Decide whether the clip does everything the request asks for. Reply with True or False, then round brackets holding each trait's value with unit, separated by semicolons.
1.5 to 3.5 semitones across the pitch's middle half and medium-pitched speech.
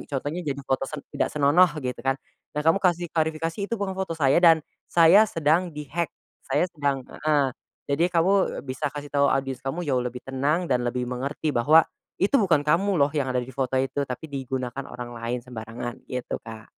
False (4.1 semitones; 145 Hz)